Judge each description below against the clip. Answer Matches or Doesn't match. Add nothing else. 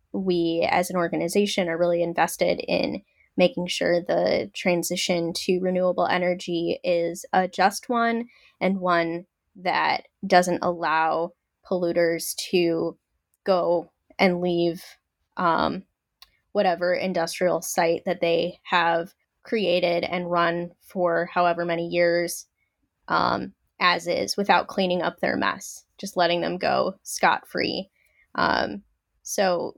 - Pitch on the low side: Doesn't match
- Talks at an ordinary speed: Doesn't match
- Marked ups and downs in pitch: Doesn't match